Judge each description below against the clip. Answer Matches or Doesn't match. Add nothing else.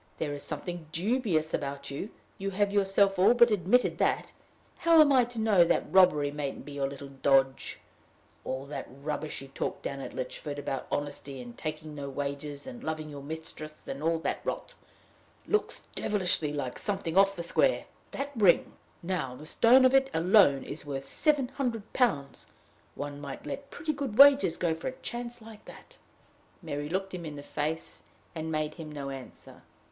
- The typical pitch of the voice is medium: Matches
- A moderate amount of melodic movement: Doesn't match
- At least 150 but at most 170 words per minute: Doesn't match